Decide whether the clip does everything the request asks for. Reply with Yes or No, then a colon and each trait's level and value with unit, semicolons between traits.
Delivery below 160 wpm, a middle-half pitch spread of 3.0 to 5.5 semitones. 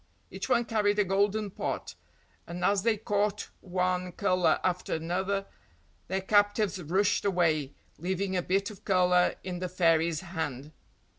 No: average, 145 wpm; narrow, 2.4 semitones